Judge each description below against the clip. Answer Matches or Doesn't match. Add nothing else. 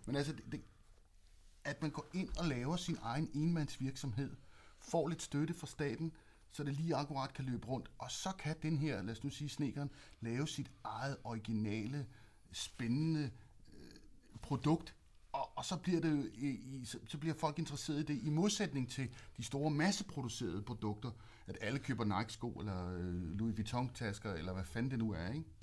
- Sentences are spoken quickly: Doesn't match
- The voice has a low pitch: Matches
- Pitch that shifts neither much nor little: Doesn't match